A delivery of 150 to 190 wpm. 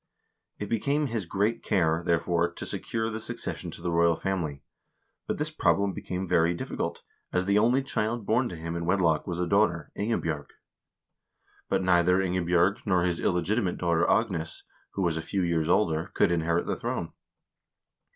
Yes: average, 170 wpm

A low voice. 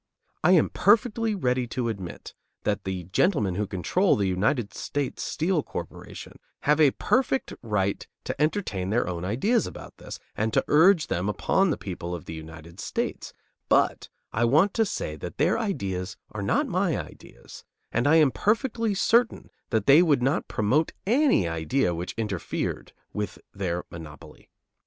Yes: low, 120 Hz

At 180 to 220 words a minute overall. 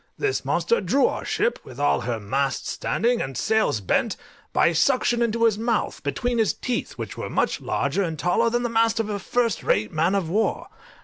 Yes: average, 200 wpm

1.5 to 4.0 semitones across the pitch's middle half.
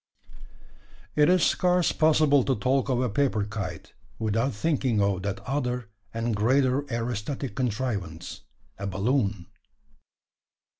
No: average, 4.9 semitones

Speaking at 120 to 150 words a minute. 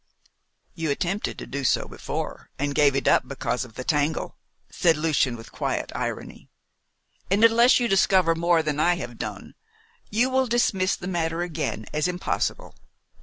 No: average, 165 wpm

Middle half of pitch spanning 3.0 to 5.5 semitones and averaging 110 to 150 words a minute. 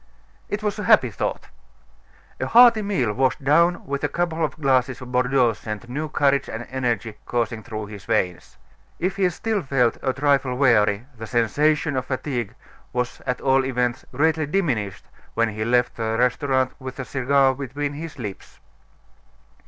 No: average, 3.7 semitones; average, 165 wpm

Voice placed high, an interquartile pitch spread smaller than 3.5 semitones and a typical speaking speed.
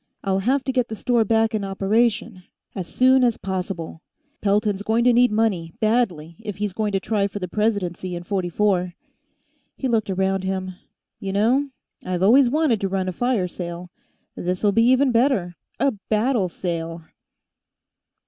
No: high, 205 Hz; average, 4.0 semitones; average, 165 wpm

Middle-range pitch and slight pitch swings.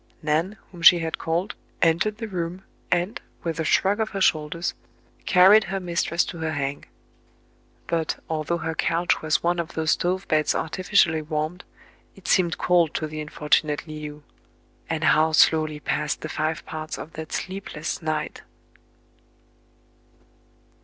Yes: medium, 165 Hz; narrow, 2.3 semitones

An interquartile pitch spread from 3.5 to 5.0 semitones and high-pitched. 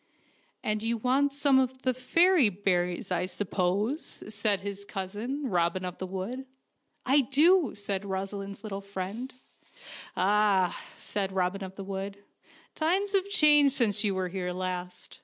No: wide, 5.6 semitones; high, 205 Hz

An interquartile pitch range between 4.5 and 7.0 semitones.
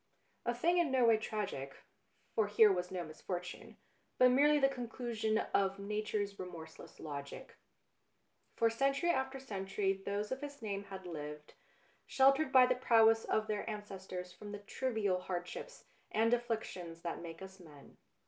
Yes: average, 5.1 semitones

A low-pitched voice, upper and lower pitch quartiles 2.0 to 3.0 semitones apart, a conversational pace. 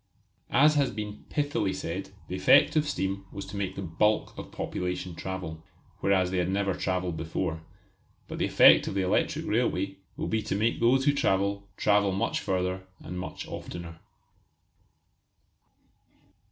Yes: very low, 95 Hz; narrow, 2.4 semitones; average, 155 wpm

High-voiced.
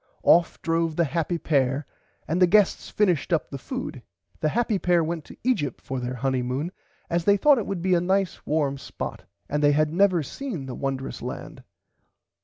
No: medium, 165 Hz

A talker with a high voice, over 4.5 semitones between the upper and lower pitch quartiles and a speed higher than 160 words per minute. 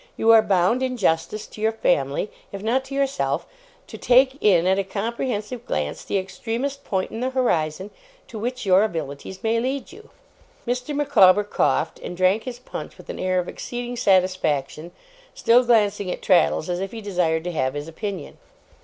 Yes: high, 205 Hz; average, 5.2 semitones; average, 180 wpm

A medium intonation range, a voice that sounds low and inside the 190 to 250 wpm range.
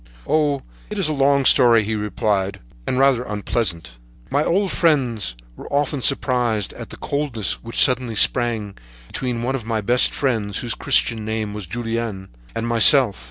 No: average, 4.0 semitones; low, 115 Hz; average, 180 wpm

